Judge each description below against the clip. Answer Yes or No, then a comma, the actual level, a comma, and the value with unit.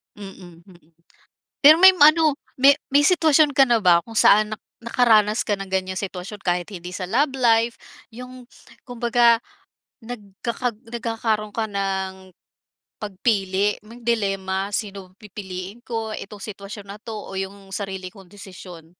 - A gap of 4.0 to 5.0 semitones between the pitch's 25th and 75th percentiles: No, average, 3.6 semitones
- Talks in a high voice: Yes, high, 210 Hz